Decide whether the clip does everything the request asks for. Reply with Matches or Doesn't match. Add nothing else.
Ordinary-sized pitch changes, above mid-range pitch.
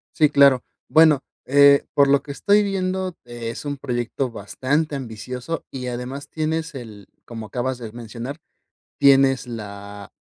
Doesn't match